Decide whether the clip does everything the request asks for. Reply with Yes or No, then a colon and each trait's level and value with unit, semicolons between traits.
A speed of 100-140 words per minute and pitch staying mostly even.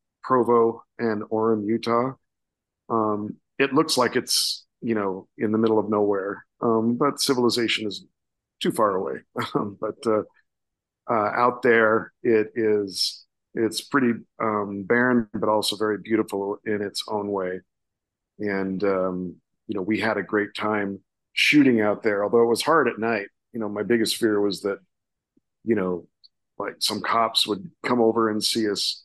No: average, 160 wpm; narrow, 2.1 semitones